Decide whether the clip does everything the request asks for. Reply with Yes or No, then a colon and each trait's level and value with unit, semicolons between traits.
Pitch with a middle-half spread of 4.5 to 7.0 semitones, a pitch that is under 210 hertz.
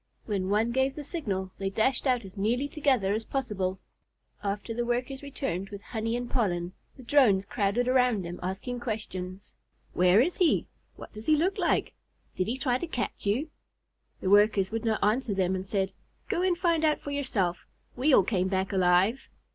No: wide, 5.4 semitones; high, 220 Hz